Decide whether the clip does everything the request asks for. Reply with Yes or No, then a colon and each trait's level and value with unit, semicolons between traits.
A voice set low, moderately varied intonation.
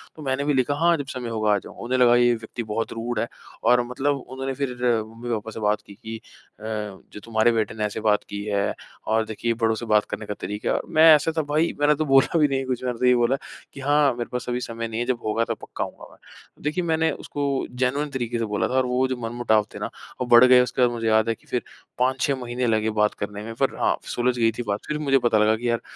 Yes: low, 120 Hz; average, 3.0 semitones